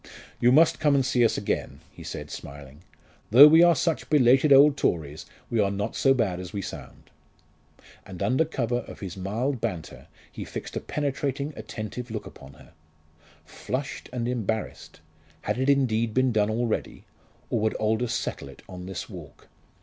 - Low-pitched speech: Yes, low, 120 Hz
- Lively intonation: No, average, 4.9 semitones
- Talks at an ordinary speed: Yes, average, 175 wpm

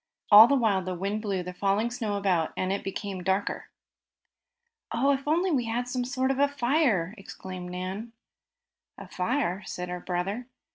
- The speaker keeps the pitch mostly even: No, average, 5.1 semitones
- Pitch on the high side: Yes, high, 205 Hz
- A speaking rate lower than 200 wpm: Yes, average, 175 wpm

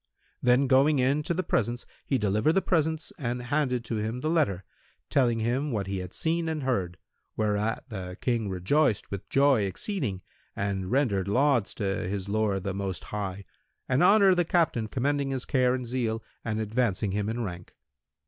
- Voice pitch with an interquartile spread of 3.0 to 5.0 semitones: No, wide, 5.6 semitones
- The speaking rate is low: No, average, 175 wpm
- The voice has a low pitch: Yes, low, 120 Hz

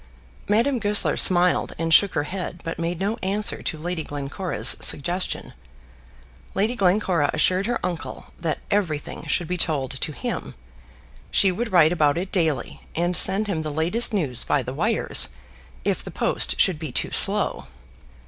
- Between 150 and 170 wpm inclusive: Yes, average, 160 wpm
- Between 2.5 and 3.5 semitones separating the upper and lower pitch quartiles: No, average, 3.9 semitones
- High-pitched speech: No, medium, 180 Hz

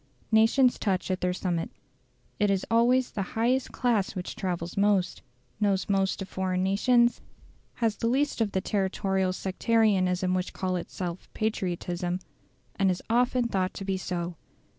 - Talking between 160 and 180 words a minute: No, average, 150 wpm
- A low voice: No, high, 195 Hz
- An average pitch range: Yes, average, 3.4 semitones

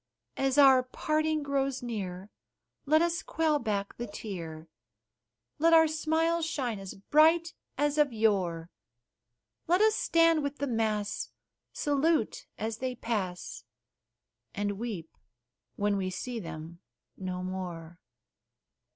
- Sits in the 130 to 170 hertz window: No, high, 240 Hz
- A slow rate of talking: Yes, slow, 120 wpm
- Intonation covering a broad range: Yes, wide, 7.9 semitones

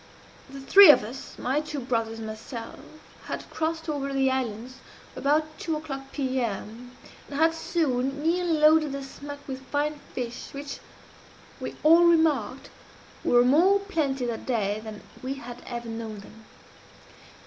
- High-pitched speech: Yes, very high, 270 Hz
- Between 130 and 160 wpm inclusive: Yes, average, 150 wpm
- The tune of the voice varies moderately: Yes, average, 4.2 semitones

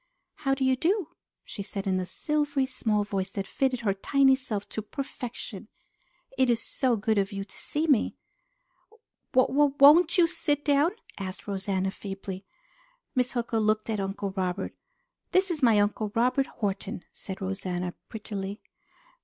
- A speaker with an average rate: Yes, average, 160 wpm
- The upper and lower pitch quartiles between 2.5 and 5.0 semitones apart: No, wide, 5.6 semitones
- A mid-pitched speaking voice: No, high, 220 Hz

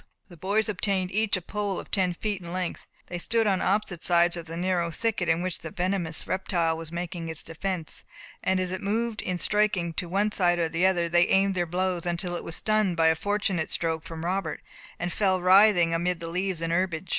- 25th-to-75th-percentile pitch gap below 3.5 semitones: Yes, narrow, 2.4 semitones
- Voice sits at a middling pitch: Yes, medium, 180 Hz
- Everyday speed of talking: No, fast, 225 wpm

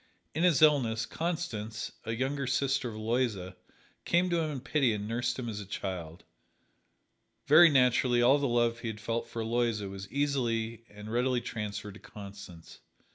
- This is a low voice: Yes, low, 120 Hz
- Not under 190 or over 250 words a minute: No, average, 170 wpm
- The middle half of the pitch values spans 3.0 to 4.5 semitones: Yes, average, 4.0 semitones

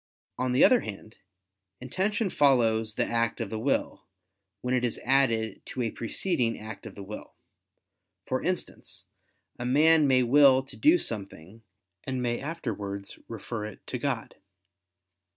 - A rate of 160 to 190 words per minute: No, average, 150 wpm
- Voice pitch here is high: No, low, 125 Hz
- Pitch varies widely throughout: No, average, 3.8 semitones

